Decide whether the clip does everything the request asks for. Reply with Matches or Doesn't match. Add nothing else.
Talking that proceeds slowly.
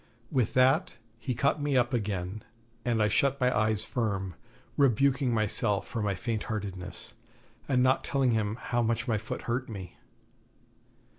Doesn't match